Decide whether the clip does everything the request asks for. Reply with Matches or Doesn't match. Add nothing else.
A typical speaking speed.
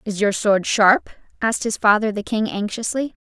Matches